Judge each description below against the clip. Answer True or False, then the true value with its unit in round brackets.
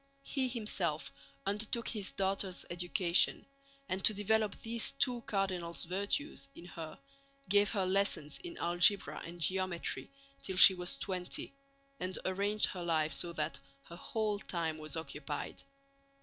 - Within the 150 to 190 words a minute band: False (135 wpm)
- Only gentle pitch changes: False (3.4 semitones)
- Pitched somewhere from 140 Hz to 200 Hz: True (190 Hz)